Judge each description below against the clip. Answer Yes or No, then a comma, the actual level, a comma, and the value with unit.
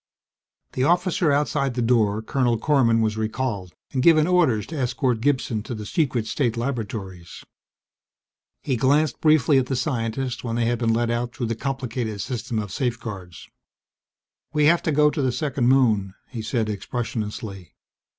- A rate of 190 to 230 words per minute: No, average, 160 wpm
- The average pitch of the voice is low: Yes, low, 120 Hz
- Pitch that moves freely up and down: No, average, 3.7 semitones